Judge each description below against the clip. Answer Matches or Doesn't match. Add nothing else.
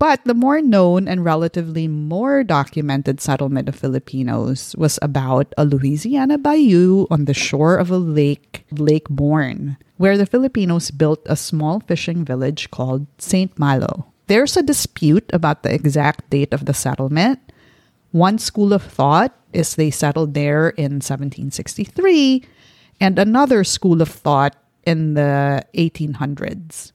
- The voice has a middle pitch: Matches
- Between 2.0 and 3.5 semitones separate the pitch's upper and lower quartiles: Doesn't match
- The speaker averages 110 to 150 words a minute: Matches